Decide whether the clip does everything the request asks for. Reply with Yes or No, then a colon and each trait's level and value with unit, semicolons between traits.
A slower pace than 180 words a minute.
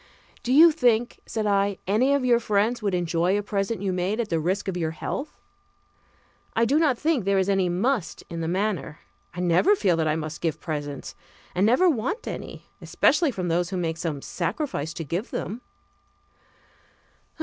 No: average, 185 wpm